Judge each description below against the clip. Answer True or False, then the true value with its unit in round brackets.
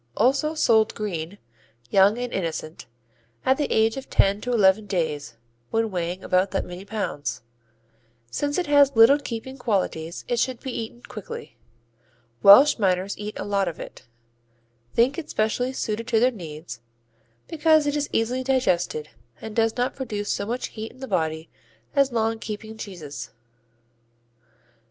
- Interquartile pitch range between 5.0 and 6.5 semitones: True (5.3 semitones)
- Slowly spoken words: False (155 wpm)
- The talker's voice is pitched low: False (220 Hz)